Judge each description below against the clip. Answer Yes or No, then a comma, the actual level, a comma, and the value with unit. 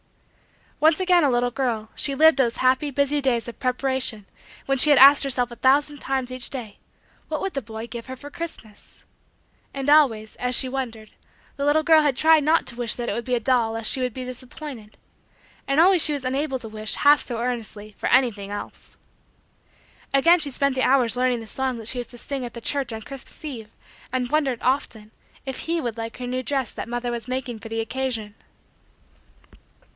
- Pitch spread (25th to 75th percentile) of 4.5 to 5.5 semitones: No, average, 3.1 semitones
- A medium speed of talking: No, fast, 210 wpm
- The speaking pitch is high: Yes, very high, 255 Hz